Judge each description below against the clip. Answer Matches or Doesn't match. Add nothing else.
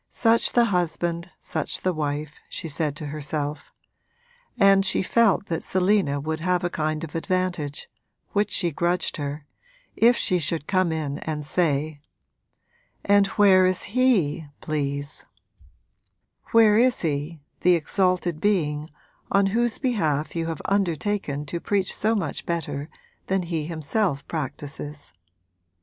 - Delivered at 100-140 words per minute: Matches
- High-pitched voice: Doesn't match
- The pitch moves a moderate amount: Matches